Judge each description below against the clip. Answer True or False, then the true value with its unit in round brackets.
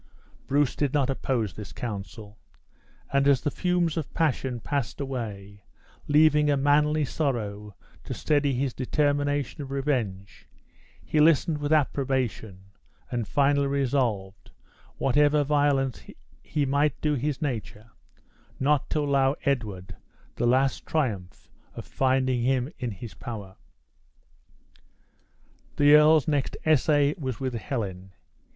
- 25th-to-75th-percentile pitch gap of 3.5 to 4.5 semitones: True (3.9 semitones)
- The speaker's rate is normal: False (120 wpm)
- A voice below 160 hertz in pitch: True (135 Hz)